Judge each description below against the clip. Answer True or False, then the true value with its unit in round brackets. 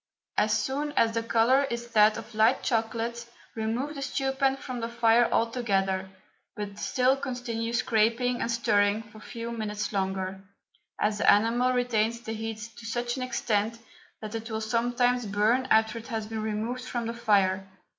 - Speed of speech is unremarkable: True (175 wpm)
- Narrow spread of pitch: True (2.1 semitones)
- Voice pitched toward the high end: True (230 Hz)